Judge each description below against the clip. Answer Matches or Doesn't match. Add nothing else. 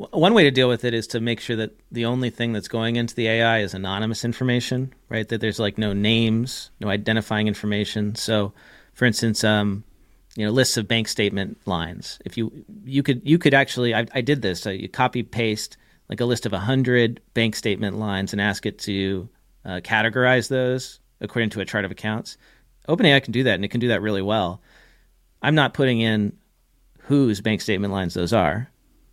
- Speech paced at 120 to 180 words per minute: Doesn't match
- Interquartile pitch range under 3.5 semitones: Matches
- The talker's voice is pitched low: Matches